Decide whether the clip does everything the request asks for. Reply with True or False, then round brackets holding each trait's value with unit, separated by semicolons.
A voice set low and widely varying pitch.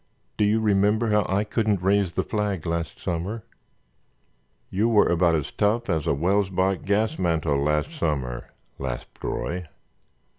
False (95 Hz; 4.1 semitones)